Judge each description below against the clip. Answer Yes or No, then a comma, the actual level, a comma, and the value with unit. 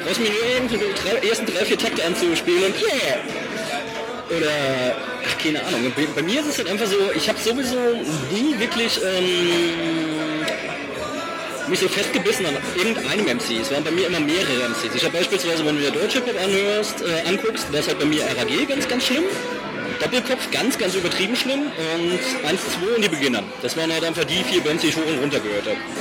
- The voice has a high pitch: Yes, high, 205 Hz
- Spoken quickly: Yes, fast, 200 wpm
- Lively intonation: Yes, wide, 7.6 semitones